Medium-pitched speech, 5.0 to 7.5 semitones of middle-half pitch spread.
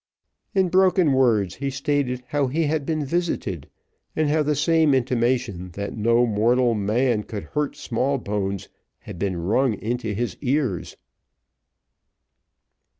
No: low, 125 Hz; wide, 5.6 semitones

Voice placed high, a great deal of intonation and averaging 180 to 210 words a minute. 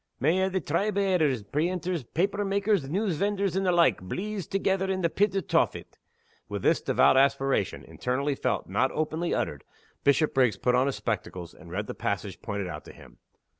No: medium, 160 Hz; wide, 7.3 semitones; average, 190 wpm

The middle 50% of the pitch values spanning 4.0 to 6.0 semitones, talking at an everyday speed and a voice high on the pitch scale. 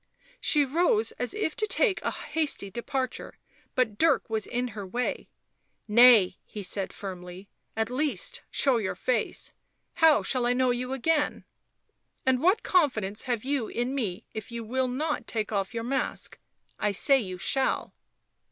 Yes: average, 4.4 semitones; average, 170 wpm; high, 245 Hz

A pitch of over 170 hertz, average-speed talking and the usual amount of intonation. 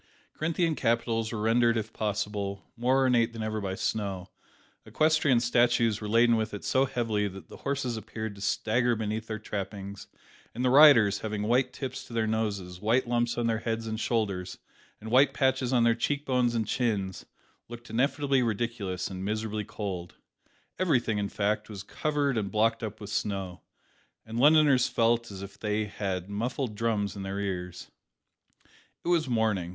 No: low, 110 Hz; average, 170 wpm; average, 3.0 semitones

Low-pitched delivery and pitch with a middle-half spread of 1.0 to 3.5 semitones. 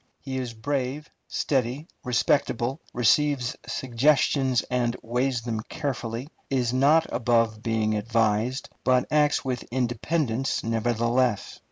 Yes: low, 125 Hz; average, 2.7 semitones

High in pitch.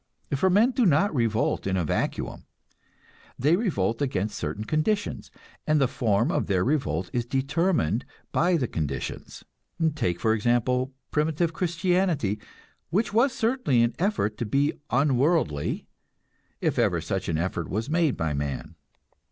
No: low, 135 Hz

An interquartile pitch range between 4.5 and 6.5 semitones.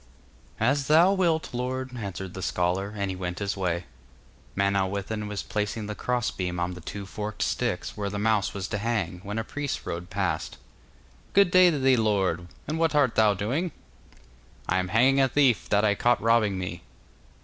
Yes: average, 5.0 semitones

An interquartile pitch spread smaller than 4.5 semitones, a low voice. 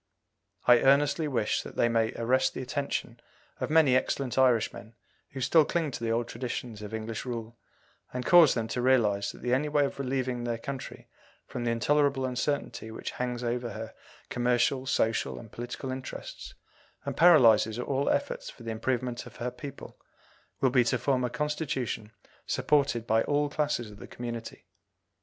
Yes: average, 2.9 semitones; low, 125 Hz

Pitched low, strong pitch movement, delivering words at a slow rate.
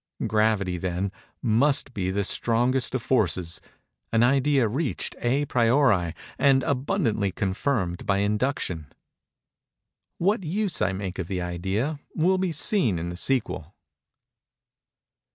Yes: low, 115 Hz; wide, 6.7 semitones; slow, 115 wpm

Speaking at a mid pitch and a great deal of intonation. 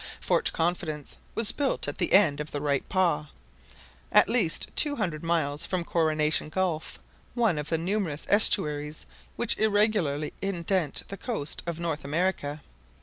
No: medium, 165 Hz; average, 4.6 semitones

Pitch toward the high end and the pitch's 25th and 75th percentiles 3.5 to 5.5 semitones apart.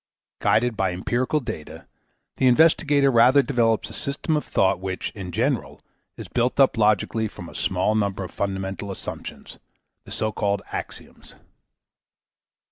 No: low, 110 Hz; average, 4.8 semitones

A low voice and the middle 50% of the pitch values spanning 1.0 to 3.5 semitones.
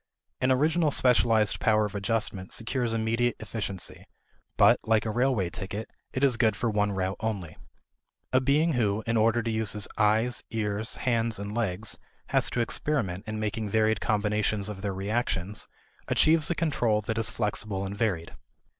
Yes: low, 110 Hz; narrow, 2.6 semitones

